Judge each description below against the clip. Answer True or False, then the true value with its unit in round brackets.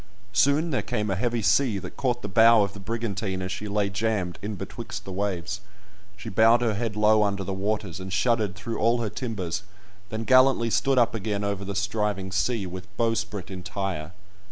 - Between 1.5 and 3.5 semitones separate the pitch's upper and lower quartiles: True (2.8 semitones)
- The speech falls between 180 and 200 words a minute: True (195 wpm)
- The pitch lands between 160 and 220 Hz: False (105 Hz)